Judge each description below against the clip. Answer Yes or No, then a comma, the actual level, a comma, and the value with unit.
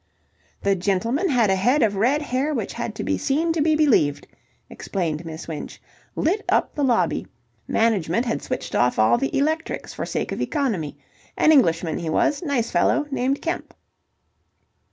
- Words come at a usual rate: Yes, average, 170 wpm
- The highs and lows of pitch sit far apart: Yes, wide, 9.0 semitones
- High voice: Yes, high, 240 Hz